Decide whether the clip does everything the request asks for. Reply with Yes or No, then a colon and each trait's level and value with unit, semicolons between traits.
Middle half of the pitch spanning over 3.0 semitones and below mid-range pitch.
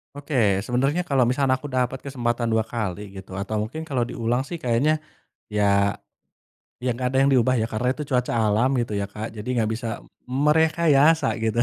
Yes: average, 3.7 semitones; low, 125 Hz